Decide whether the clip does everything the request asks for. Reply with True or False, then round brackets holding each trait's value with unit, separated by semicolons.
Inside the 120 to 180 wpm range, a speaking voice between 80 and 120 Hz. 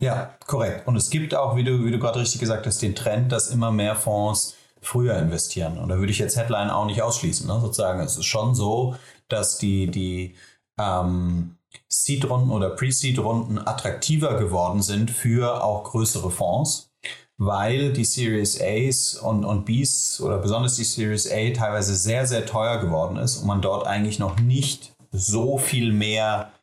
True (175 wpm; 110 Hz)